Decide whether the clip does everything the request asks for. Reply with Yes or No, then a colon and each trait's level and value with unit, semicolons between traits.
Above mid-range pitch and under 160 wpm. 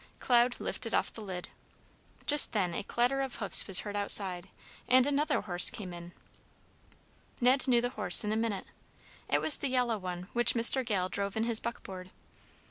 No: high, 220 Hz; average, 180 wpm